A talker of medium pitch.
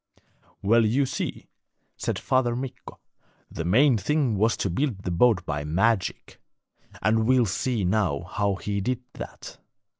No: low, 110 Hz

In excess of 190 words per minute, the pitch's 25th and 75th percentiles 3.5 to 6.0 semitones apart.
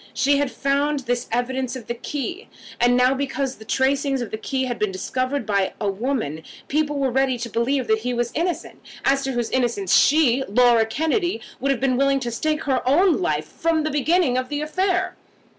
No: fast, 205 wpm; average, 3.1 semitones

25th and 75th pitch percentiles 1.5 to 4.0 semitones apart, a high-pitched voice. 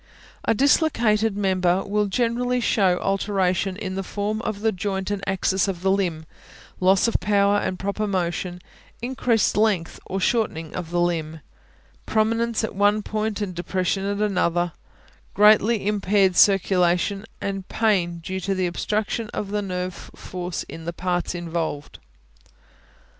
Yes: average, 2.8 semitones; high, 195 Hz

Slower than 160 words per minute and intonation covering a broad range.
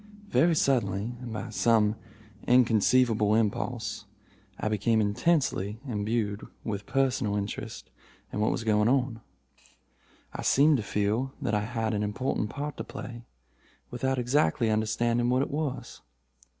No: slow, 135 wpm; average, 3.3 semitones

